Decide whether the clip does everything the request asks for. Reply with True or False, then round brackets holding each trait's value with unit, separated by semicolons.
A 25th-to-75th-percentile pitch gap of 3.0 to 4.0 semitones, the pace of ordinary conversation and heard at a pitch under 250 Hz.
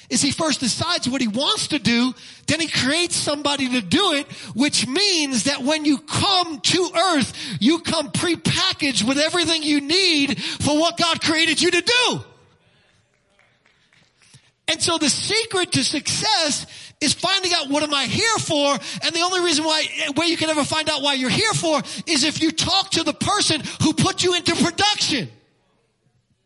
False (3.5 semitones; 180 wpm; 310 Hz)